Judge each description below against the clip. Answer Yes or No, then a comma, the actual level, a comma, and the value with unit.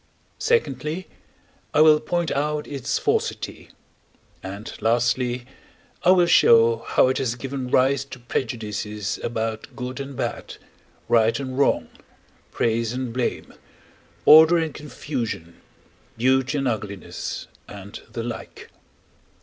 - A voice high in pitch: No, low, 125 Hz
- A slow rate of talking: Yes, slow, 115 wpm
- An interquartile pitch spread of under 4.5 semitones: Yes, average, 3.7 semitones